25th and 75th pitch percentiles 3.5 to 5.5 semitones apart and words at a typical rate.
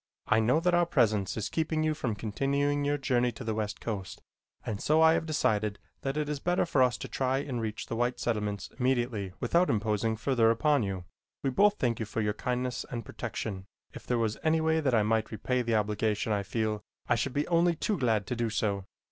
No: average, 4.9 semitones; fast, 225 wpm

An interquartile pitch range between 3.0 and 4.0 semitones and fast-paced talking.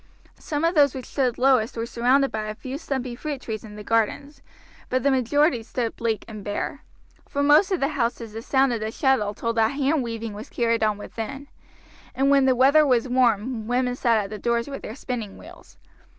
Yes: average, 3.5 semitones; fast, 210 wpm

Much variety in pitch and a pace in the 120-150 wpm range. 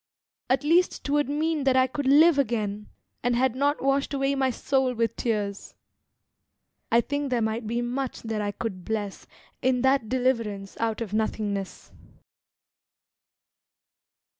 No: average, 3.8 semitones; average, 140 wpm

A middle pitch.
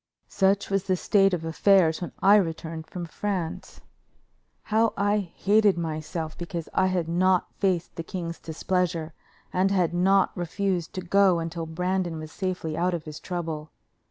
Yes: medium, 180 Hz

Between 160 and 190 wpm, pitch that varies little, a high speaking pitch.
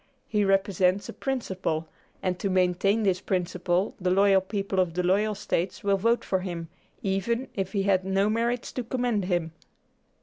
Yes: average, 170 wpm; narrow, 2.3 semitones; high, 195 Hz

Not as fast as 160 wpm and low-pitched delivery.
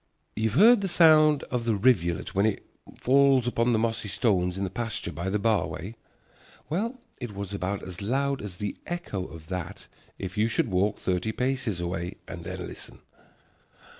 No: average, 185 wpm; low, 105 Hz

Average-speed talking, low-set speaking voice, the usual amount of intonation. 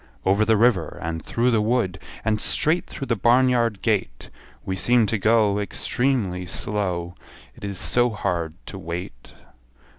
Yes: average, 155 wpm; low, 105 Hz; average, 4.3 semitones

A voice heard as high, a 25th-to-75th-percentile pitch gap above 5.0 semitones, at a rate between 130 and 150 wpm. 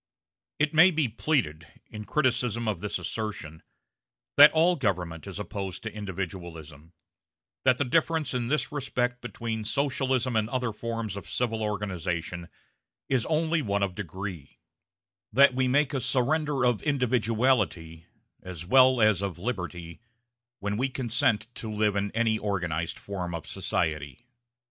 No: low, 110 Hz; wide, 5.5 semitones; average, 140 wpm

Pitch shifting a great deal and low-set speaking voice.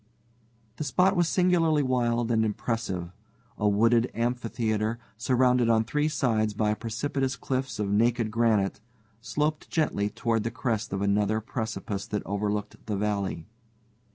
No: average, 3.3 semitones; low, 115 Hz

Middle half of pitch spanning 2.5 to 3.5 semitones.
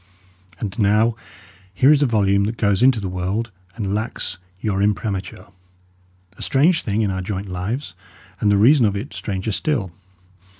Yes: average, 3.0 semitones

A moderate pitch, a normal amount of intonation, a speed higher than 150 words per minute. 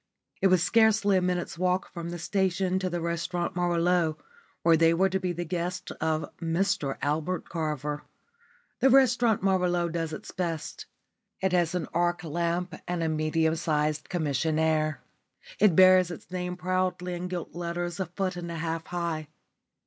No: medium, 175 Hz; narrow, 2.0 semitones; average, 165 wpm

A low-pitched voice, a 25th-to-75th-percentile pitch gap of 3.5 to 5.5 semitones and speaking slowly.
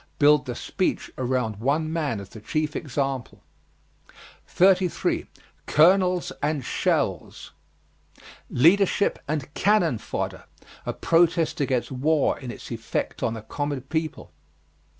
No: medium, 145 Hz; average, 4.5 semitones; slow, 115 wpm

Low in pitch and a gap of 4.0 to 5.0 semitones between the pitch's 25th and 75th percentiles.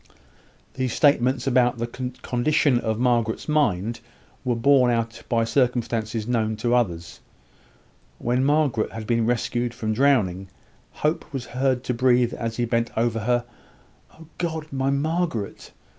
No: low, 120 Hz; narrow, 2.6 semitones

